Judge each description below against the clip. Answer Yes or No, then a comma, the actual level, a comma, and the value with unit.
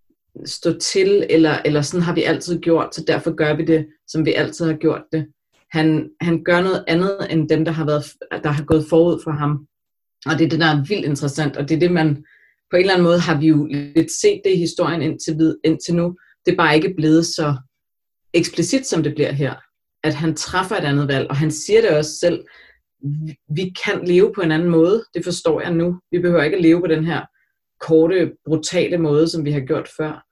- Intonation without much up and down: Yes, narrow, 2.0 semitones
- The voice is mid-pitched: Yes, medium, 160 Hz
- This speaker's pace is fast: Yes, fast, 230 wpm